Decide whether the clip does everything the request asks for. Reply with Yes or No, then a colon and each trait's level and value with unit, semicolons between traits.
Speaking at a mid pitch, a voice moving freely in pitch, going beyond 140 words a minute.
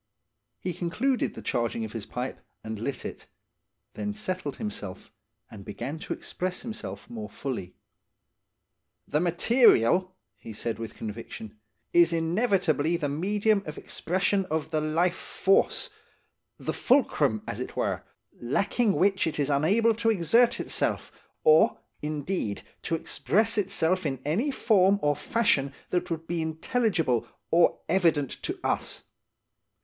No: medium, 170 Hz; wide, 6.2 semitones; slow, 135 wpm